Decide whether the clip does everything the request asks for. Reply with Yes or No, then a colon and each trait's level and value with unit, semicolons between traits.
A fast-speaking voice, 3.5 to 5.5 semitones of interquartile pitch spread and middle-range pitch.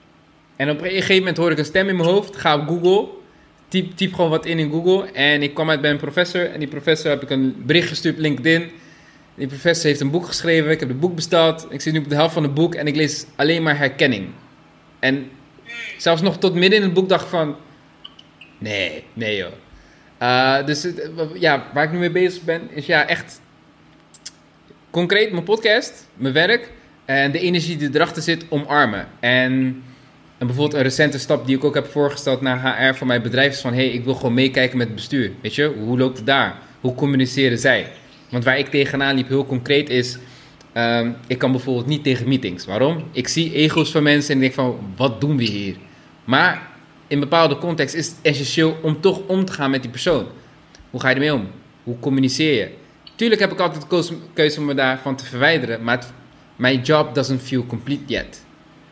Yes: fast, 210 wpm; average, 3.9 semitones; medium, 145 Hz